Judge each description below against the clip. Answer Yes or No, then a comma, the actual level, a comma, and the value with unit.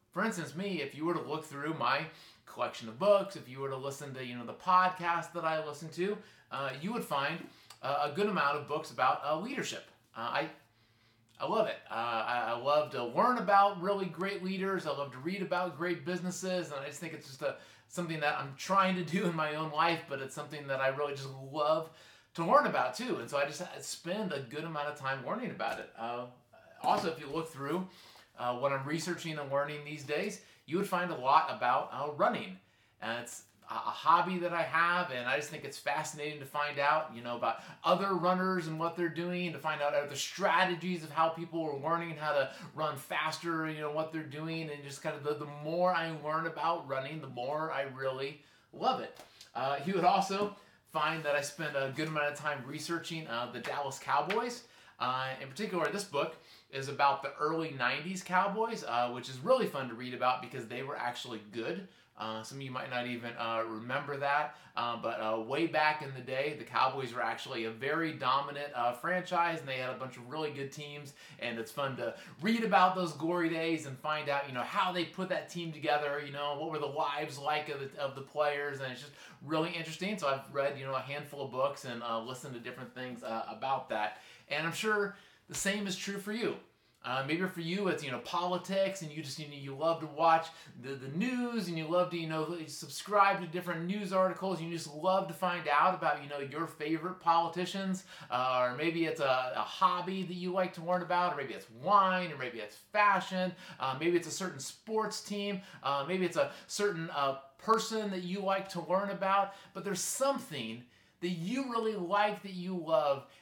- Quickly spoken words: Yes, fast, 225 wpm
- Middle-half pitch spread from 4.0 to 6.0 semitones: Yes, average, 4.8 semitones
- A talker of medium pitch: Yes, medium, 155 Hz